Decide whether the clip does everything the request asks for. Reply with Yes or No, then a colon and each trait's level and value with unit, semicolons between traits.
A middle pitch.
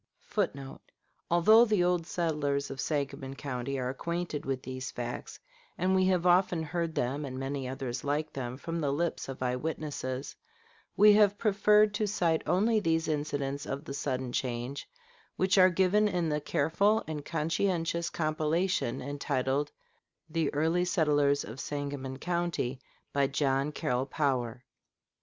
Yes: medium, 150 Hz